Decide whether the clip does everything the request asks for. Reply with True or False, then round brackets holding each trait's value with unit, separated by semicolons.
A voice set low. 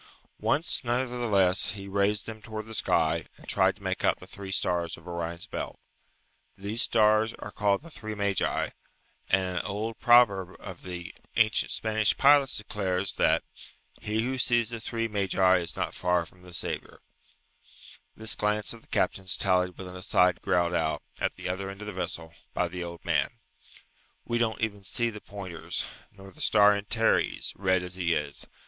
True (100 Hz)